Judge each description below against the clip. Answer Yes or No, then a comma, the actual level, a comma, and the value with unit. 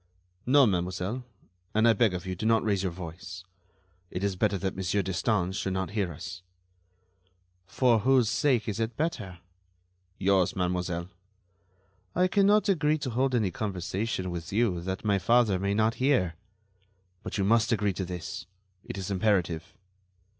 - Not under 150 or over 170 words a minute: Yes, average, 160 wpm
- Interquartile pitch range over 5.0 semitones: No, average, 4.1 semitones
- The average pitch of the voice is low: Yes, low, 100 Hz